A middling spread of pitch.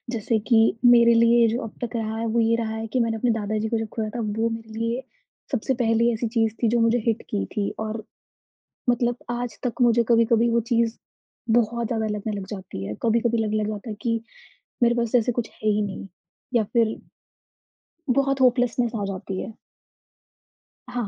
No: narrow, 1.5 semitones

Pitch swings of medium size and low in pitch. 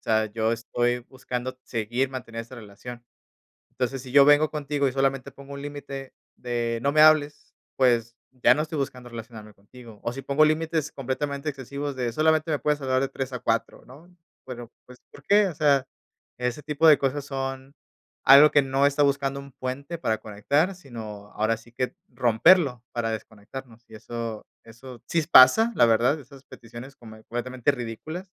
Yes: average, 3.4 semitones; low, 130 Hz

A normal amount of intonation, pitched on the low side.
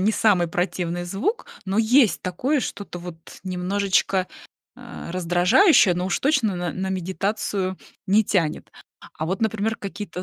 No: average, 3.3 semitones; high, 190 Hz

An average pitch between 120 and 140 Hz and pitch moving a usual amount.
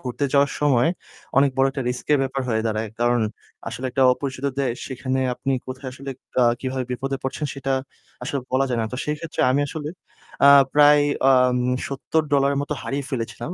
No: low, 135 Hz; narrow, 1.9 semitones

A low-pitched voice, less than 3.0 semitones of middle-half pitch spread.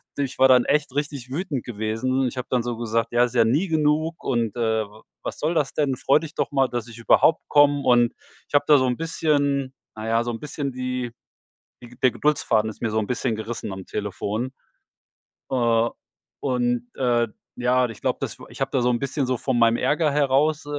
No: low, 125 Hz; average, 3.4 semitones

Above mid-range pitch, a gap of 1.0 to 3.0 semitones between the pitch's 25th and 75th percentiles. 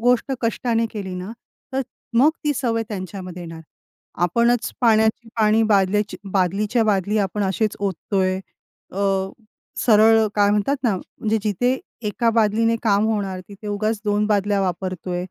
Yes: high, 210 Hz; average, 2.7 semitones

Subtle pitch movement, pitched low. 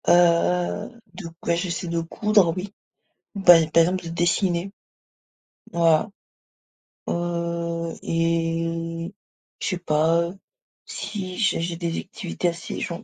No: narrow, 1.2 semitones; medium, 170 Hz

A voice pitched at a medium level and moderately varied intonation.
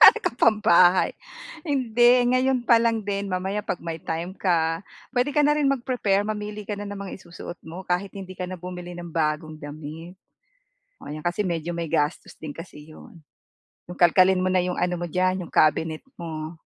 Yes: medium, 180 Hz; average, 4.0 semitones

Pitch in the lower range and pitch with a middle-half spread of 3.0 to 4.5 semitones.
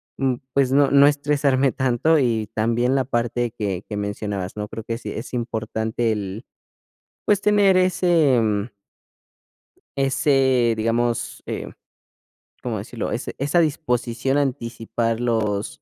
Yes: low, 120 Hz; average, 3.7 semitones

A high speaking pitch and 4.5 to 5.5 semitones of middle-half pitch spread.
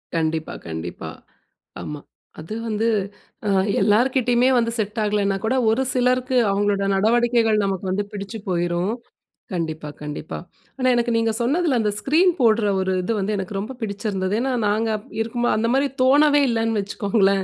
No: high, 215 Hz; average, 3.6 semitones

